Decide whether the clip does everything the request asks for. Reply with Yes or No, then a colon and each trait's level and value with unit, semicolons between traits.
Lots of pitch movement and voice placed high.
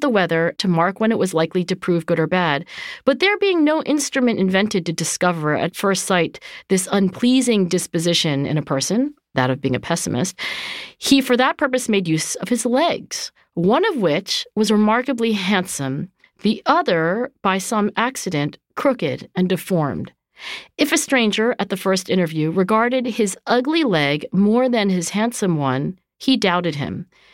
Yes: wide, 6.2 semitones; high, 195 Hz